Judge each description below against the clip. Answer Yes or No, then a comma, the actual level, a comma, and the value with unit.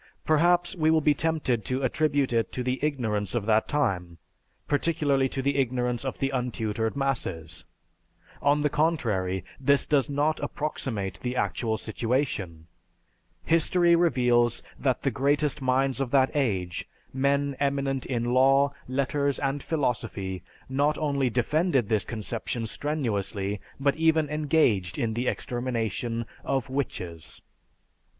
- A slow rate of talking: Yes, slow, 130 wpm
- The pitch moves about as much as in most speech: Yes, average, 4.0 semitones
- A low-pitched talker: Yes, low, 130 Hz